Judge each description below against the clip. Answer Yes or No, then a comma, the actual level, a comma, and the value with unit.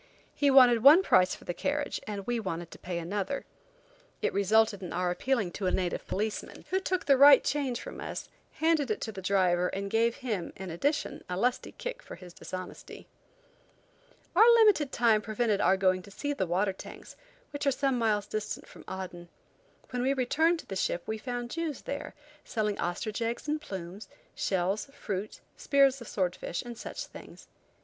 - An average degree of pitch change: No, wide, 6.5 semitones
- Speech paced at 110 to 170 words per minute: No, average, 190 wpm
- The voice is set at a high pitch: Yes, high, 220 Hz